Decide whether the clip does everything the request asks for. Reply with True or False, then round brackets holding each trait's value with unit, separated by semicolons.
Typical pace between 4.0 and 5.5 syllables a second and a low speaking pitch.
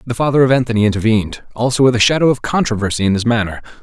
False (7.7 syllables/s; 120 Hz)